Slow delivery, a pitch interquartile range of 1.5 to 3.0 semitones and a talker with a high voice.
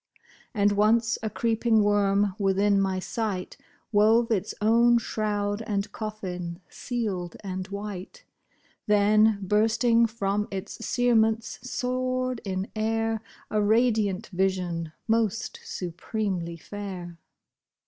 Yes: slow, 105 wpm; narrow, 2.5 semitones; high, 210 Hz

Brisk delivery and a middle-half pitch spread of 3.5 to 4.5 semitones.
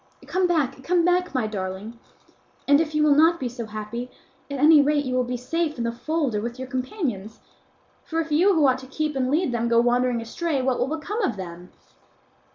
No: fast, 220 wpm; average, 4.9 semitones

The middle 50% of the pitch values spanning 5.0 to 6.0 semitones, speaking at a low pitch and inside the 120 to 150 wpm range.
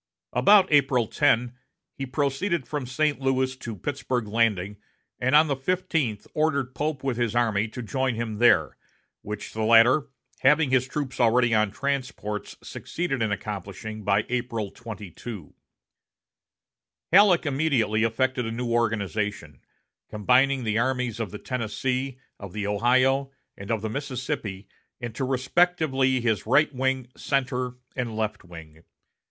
No: average, 3.8 semitones; low, 125 Hz; slow, 135 wpm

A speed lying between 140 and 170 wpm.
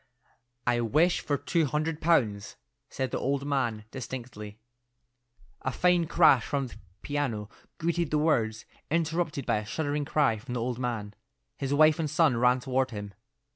Yes: average, 160 wpm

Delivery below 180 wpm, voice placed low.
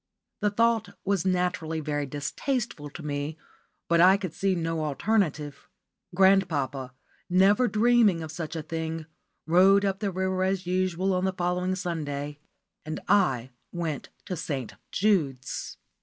No: average, 140 wpm; medium, 175 Hz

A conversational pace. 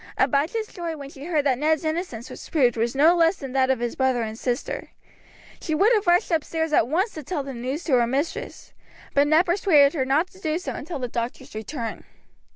No: fast, 220 wpm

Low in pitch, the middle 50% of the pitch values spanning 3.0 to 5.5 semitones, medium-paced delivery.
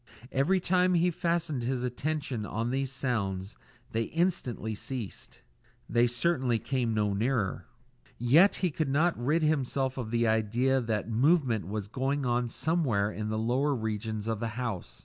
Yes: low, 125 Hz; average, 4.5 semitones; average, 155 wpm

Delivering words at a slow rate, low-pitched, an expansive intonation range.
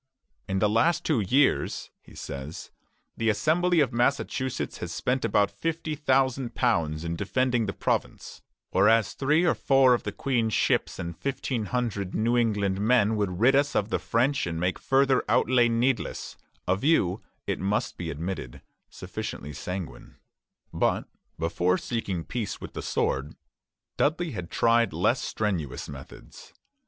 No: average, 145 wpm; low, 115 Hz; wide, 5.8 semitones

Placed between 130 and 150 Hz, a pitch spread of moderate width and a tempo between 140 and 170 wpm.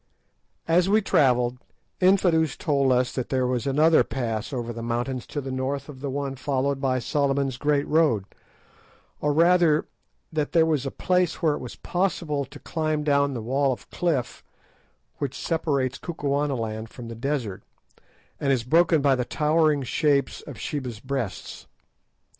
Yes: medium, 140 Hz; average, 3.3 semitones; average, 160 wpm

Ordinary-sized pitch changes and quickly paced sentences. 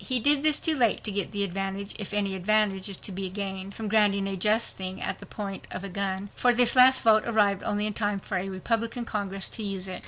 No: narrow, 2.3 semitones; fast, 240 wpm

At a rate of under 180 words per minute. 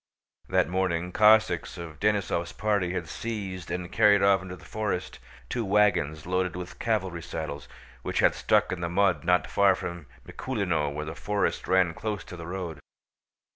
Yes: average, 170 wpm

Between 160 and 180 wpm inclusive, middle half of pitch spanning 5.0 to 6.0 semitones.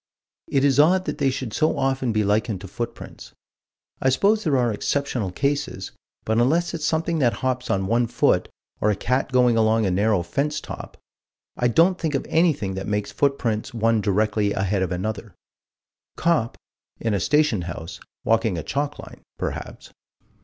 Yes: average, 175 wpm; wide, 5.5 semitones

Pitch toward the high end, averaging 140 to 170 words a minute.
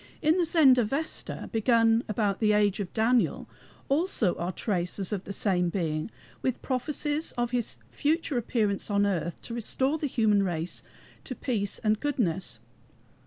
Yes: high, 220 Hz; average, 150 wpm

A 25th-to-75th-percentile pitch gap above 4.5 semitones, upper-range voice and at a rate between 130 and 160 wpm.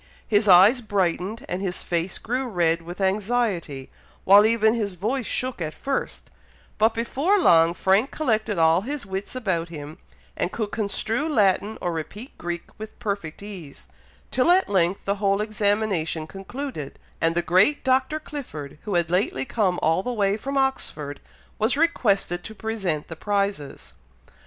Yes: average, 5.0 semitones; high, 200 Hz; average, 155 wpm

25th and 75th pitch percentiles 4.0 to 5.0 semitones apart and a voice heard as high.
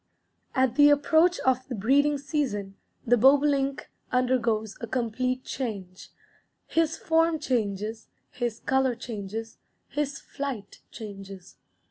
Yes: average, 4.5 semitones; very high, 255 Hz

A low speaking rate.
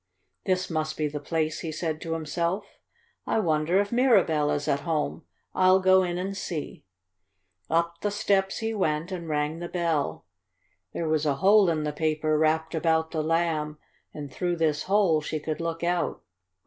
No: average, 175 wpm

